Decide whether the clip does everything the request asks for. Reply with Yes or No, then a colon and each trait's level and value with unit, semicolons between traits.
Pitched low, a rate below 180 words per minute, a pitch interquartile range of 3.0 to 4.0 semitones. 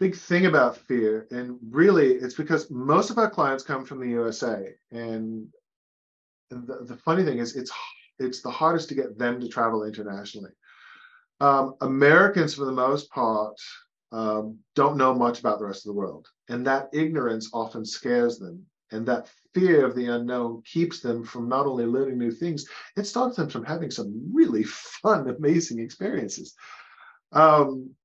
No: low, 130 Hz; average, 170 wpm; average, 5.2 semitones